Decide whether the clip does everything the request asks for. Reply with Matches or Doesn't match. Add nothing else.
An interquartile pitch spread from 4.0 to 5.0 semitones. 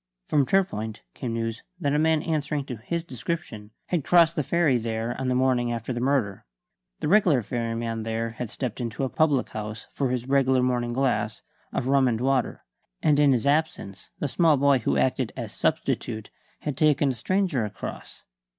Matches